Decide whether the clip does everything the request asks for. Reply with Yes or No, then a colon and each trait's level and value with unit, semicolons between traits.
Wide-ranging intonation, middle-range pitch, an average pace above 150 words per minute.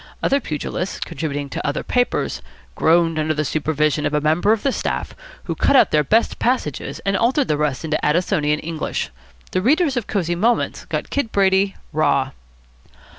Yes: wide, 6.4 semitones; medium, 165 Hz; average, 175 wpm